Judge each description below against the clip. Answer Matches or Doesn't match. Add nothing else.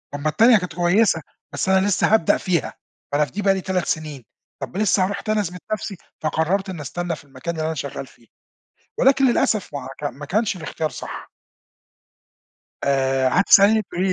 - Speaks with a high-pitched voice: Doesn't match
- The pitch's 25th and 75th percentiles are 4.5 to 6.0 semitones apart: Matches